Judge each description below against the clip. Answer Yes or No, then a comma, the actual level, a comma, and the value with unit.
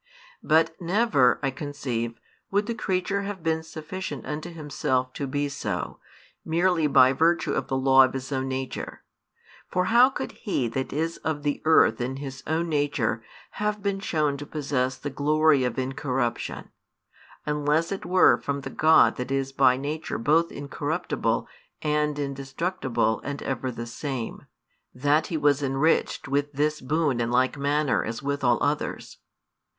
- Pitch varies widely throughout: No, average, 3.3 semitones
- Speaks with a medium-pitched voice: Yes, medium, 145 Hz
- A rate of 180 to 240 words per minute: No, average, 160 wpm